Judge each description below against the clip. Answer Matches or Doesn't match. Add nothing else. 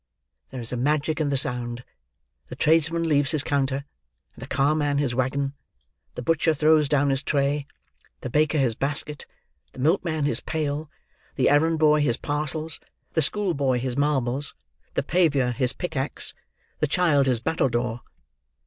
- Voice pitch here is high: Doesn't match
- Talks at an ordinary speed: Matches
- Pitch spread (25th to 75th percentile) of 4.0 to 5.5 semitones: Doesn't match